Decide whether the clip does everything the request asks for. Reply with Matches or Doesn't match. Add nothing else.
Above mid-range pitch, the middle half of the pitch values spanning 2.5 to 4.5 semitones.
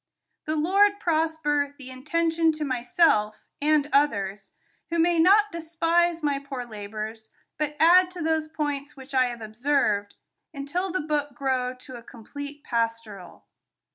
Doesn't match